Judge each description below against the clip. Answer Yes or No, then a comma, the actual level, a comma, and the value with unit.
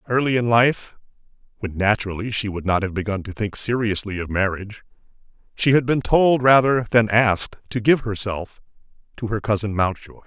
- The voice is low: Yes, low, 110 Hz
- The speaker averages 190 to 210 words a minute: No, average, 170 wpm